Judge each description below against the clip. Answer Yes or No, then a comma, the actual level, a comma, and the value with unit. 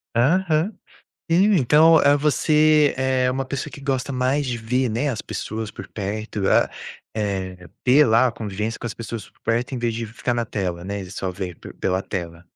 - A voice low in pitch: Yes, low, 120 Hz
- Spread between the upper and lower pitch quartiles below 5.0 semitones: No, average, 5.3 semitones